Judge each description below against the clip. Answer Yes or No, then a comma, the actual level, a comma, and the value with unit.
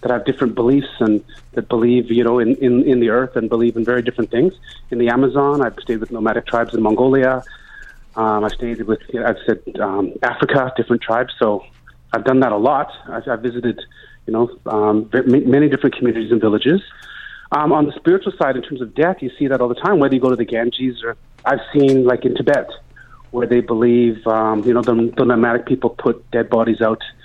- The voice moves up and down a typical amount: No, narrow, 2.0 semitones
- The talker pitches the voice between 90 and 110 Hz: No, low, 120 Hz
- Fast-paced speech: Yes, fast, 220 wpm